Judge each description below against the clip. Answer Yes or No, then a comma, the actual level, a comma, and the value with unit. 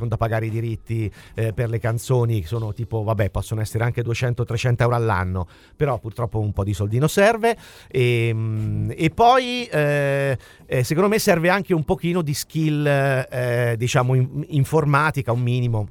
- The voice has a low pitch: Yes, low, 120 Hz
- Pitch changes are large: No, average, 4.7 semitones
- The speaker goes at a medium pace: Yes, average, 160 wpm